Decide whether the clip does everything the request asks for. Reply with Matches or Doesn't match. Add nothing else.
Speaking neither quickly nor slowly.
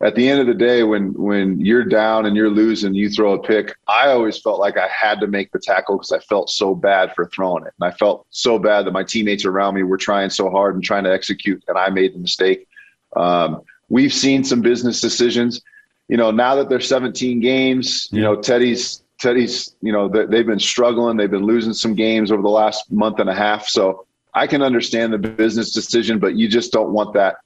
Doesn't match